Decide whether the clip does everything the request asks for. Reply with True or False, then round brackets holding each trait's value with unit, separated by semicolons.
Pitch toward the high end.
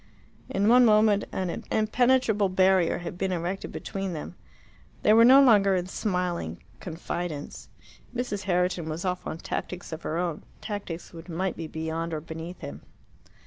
False (180 Hz)